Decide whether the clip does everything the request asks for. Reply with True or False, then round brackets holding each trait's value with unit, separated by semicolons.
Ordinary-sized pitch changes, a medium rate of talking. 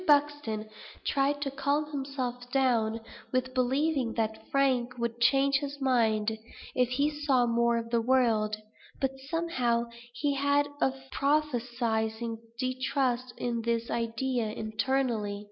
False (3.1 semitones; 125 wpm)